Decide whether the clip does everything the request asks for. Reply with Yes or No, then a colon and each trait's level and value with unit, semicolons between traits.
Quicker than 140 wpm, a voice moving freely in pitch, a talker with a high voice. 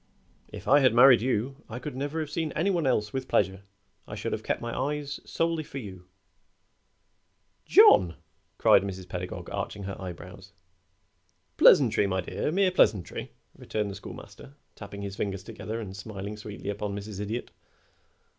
No: average, 160 wpm; wide, 5.7 semitones; low, 105 Hz